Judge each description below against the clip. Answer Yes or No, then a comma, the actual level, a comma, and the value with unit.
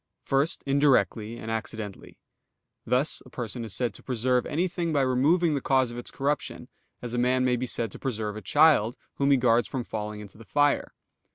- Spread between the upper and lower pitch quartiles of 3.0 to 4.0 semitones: Yes, average, 3.7 semitones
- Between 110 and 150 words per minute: No, average, 195 wpm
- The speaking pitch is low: Yes, low, 125 Hz